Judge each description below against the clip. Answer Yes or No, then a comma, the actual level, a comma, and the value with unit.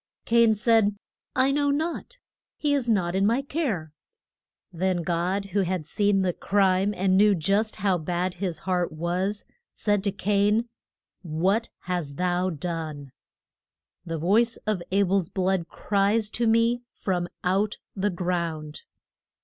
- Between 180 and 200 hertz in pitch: Yes, high, 190 Hz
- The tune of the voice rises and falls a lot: No, average, 3.3 semitones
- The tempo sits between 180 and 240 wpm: No, average, 140 wpm